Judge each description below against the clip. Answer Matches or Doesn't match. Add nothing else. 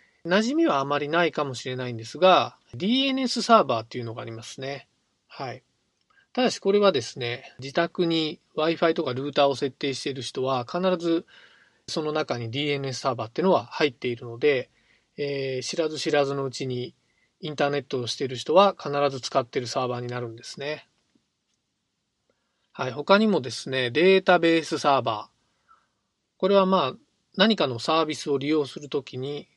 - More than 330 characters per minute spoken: Matches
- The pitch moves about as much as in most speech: Matches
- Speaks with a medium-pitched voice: Matches